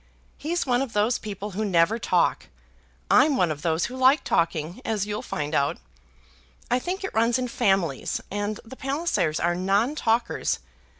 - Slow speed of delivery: No, average, 170 wpm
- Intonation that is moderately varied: No, wide, 6.5 semitones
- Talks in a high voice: Yes, high, 215 Hz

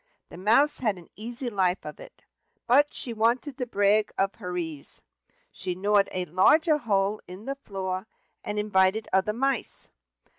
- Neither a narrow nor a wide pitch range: Yes, average, 4.3 semitones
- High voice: Yes, high, 210 Hz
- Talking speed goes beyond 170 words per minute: No, average, 160 wpm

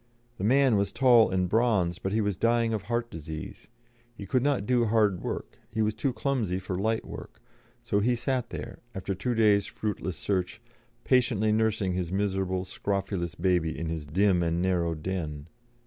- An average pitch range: Yes, average, 3.9 semitones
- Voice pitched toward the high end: No, low, 100 Hz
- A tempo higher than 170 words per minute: Yes, average, 180 wpm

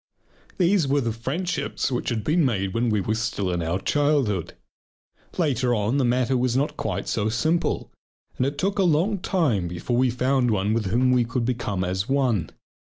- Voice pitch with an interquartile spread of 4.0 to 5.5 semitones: Yes, average, 4.9 semitones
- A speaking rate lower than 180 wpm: No, average, 185 wpm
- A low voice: Yes, low, 125 Hz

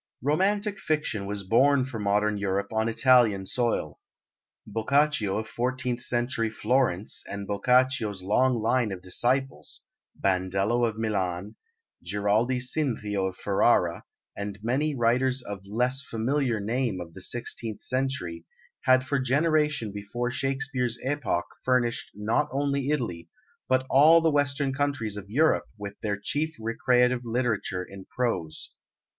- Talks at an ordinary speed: No, slow, 130 wpm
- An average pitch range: Yes, average, 4.5 semitones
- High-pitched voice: No, low, 120 Hz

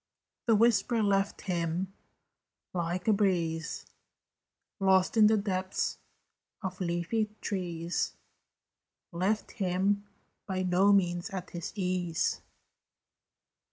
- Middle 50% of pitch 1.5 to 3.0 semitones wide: Yes, narrow, 2.5 semitones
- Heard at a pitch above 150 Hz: Yes, medium, 185 Hz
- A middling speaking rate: No, slow, 95 wpm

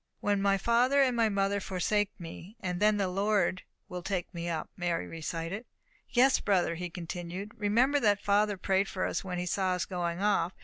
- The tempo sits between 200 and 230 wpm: No, average, 185 wpm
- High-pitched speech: Yes, high, 195 Hz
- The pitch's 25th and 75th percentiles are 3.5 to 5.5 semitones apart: No, average, 2.7 semitones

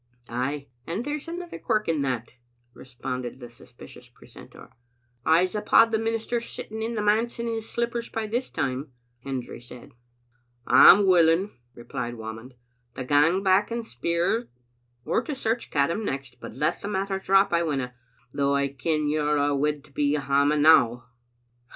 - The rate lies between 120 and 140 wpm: No, average, 160 wpm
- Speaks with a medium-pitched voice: Yes, medium, 155 Hz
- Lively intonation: Yes, wide, 8.2 semitones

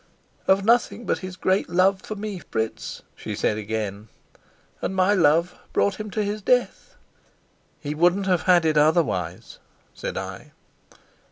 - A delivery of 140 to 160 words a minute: Yes, average, 150 wpm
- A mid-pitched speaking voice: Yes, medium, 180 Hz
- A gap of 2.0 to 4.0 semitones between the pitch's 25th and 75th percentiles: No, average, 5.3 semitones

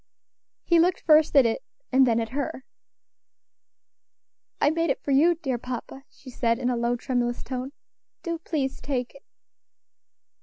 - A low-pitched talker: No, very high, 265 Hz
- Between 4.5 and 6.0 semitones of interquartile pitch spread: No, average, 3.8 semitones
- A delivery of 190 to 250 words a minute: No, average, 155 wpm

